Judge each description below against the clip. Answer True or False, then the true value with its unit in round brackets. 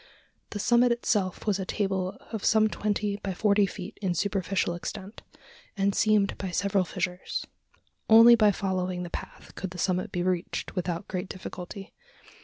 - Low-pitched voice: False (195 Hz)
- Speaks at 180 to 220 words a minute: False (160 wpm)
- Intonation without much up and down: True (2.3 semitones)